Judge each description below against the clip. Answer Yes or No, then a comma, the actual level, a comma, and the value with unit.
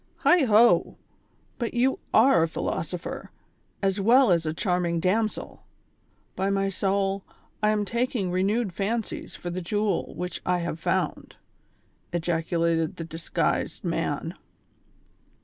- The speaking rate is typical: No, slow, 125 wpm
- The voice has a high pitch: Yes, high, 195 Hz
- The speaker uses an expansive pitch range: No, average, 4.0 semitones